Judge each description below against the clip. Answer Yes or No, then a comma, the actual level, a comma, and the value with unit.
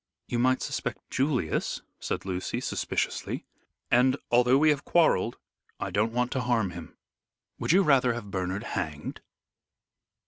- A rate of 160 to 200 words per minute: No, average, 140 wpm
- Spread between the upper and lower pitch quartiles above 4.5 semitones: Yes, average, 5.1 semitones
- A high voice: No, low, 120 Hz